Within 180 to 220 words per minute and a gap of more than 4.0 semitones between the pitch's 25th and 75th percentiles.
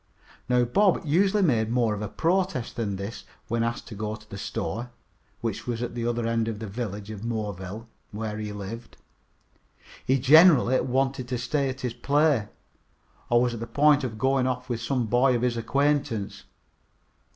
No: average, 185 wpm; average, 3.3 semitones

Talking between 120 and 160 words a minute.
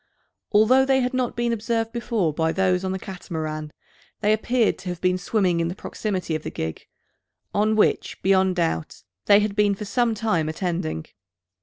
No: average, 180 wpm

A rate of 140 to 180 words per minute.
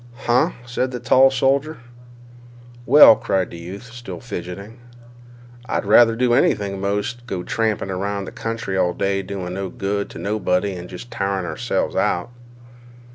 Yes: average, 155 wpm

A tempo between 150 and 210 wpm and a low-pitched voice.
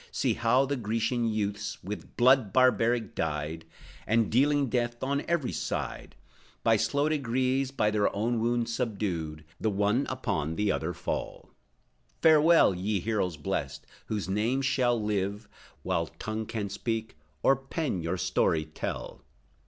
No: average, 140 wpm; low, 110 Hz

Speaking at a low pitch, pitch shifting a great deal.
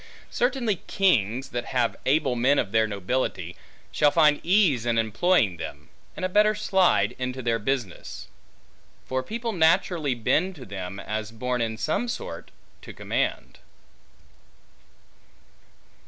Yes: low, 130 Hz; wide, 8.4 semitones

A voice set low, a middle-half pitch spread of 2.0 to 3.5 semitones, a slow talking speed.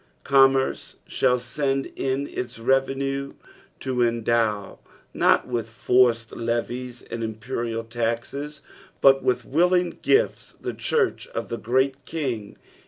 Yes: low, 125 Hz; average, 2.8 semitones; slow, 115 wpm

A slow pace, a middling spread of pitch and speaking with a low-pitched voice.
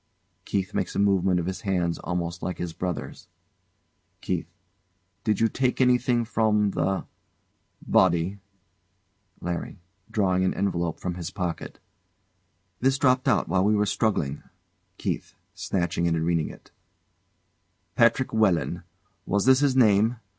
Yes: slow, 130 wpm; average, 4.1 semitones; very low, 95 Hz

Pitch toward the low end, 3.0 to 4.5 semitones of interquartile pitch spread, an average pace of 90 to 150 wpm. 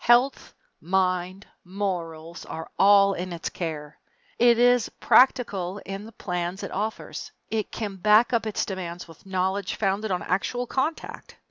No: high, 195 Hz; average, 3.6 semitones; average, 145 wpm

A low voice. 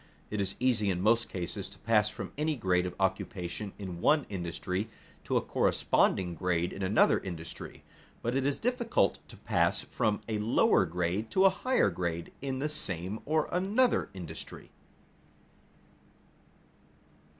Yes: low, 105 Hz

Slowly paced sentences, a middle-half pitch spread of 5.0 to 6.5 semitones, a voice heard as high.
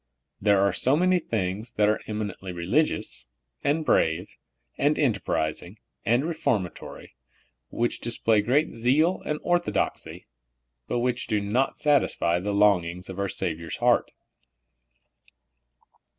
No: slow, 120 wpm; wide, 5.5 semitones; low, 110 Hz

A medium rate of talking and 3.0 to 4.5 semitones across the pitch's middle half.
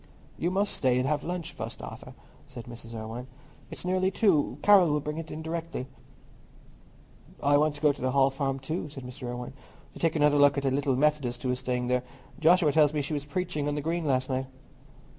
No: fast, 215 wpm; average, 3.7 semitones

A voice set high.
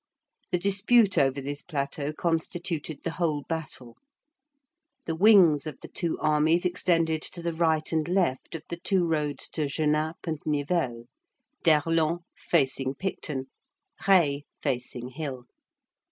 No: medium, 160 Hz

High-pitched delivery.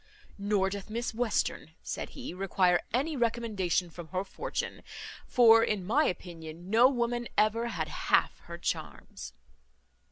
Yes: high, 215 Hz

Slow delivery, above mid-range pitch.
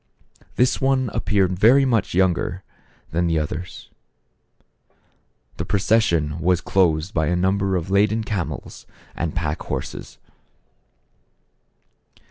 No: slow, 110 wpm; very low, 95 Hz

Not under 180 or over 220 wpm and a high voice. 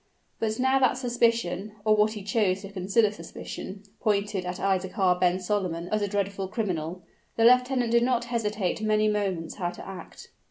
No: average, 170 wpm; high, 205 Hz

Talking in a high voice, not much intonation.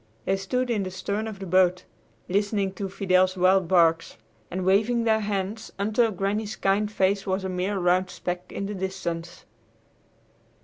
Yes: high, 195 Hz; narrow, 2.0 semitones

